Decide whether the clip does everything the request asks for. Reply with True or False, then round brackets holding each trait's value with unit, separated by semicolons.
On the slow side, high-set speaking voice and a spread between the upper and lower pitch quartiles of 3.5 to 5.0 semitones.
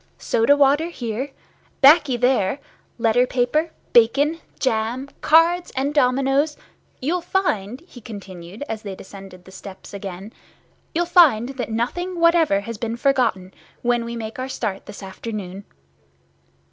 False (125 wpm; 245 Hz; 5.4 semitones)